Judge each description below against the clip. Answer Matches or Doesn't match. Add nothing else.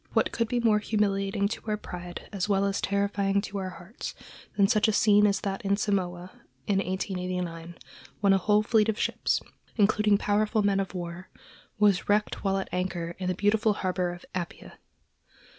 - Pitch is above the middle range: Matches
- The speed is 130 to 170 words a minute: Doesn't match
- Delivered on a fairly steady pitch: Matches